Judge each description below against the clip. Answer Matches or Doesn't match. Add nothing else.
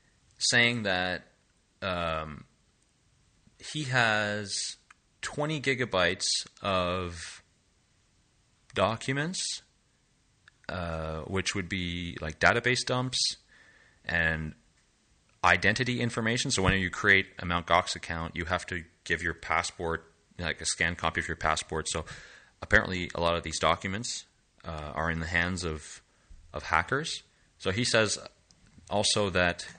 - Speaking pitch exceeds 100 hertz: Doesn't match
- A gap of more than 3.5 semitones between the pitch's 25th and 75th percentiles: Matches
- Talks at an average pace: Doesn't match